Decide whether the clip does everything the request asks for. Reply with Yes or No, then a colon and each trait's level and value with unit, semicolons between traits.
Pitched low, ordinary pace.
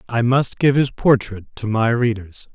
Yes: low, 120 Hz; average, 190 wpm